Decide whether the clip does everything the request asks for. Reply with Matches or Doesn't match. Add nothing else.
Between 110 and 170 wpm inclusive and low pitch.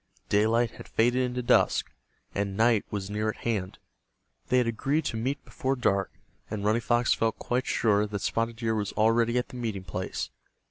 Doesn't match